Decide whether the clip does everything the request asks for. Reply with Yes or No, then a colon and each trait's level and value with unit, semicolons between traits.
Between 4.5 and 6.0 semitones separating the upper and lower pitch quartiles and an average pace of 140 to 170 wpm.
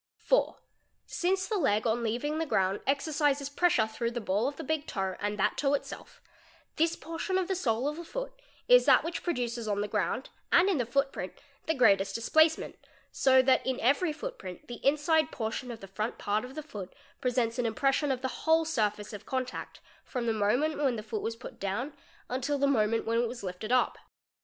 No: wide, 5.6 semitones; fast, 205 wpm